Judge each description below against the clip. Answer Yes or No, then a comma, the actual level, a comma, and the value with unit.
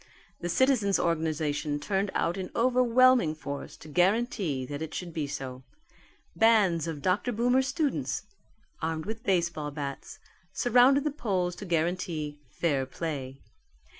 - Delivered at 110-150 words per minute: Yes, slow, 135 wpm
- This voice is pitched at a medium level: Yes, medium, 175 Hz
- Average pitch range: No, wide, 7.1 semitones